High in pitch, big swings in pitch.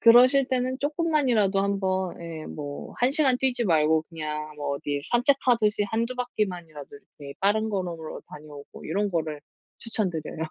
Yes: high, 195 Hz; wide, 7.7 semitones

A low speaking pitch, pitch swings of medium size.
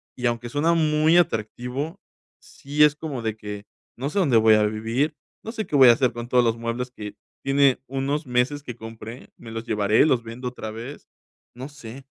Yes: low, 125 Hz; average, 4.2 semitones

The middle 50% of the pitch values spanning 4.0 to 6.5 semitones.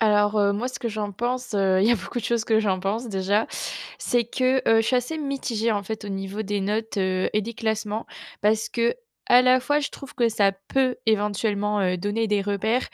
No: average, 2.8 semitones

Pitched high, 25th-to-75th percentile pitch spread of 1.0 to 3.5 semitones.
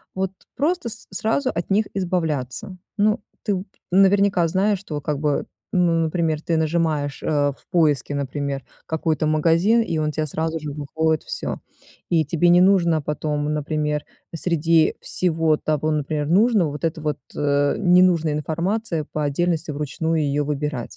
No: medium, 160 Hz; average, 3.2 semitones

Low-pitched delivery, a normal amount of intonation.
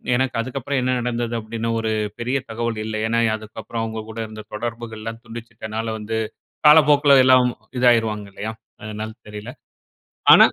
No: low, 115 Hz; narrow, 1.9 semitones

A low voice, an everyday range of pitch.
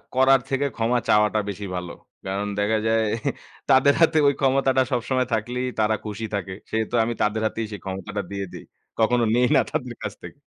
Yes: low, 110 Hz; average, 3.7 semitones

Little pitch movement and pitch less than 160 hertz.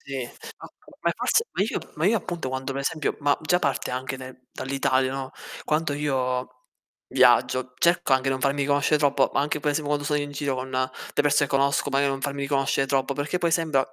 Yes: narrow, 1.9 semitones; medium, 140 Hz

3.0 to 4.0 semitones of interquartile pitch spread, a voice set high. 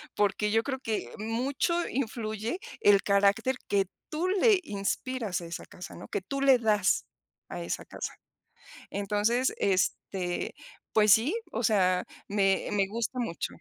No: average, 4.4 semitones; high, 215 Hz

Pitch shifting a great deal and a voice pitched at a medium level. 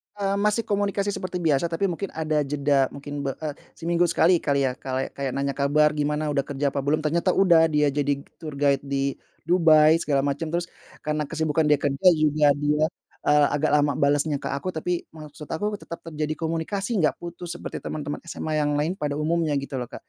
No: average, 2.7 semitones; medium, 150 Hz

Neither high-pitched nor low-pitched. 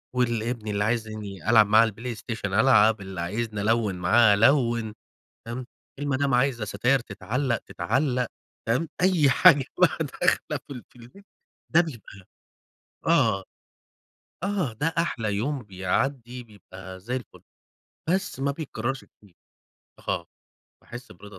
No: low, 115 Hz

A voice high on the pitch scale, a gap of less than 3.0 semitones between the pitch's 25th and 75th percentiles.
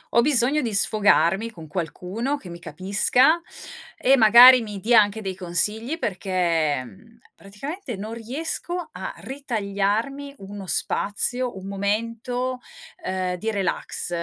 No: high, 215 Hz; average, 4.7 semitones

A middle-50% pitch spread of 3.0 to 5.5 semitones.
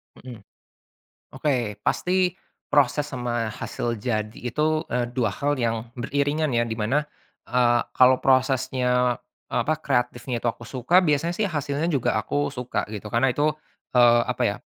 Yes: average, 3.4 semitones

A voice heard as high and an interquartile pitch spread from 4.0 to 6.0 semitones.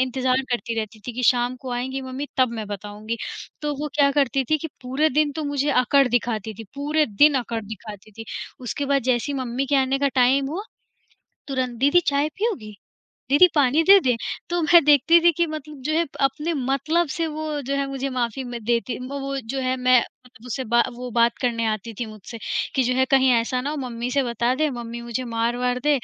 No: very high, 260 Hz; average, 3.2 semitones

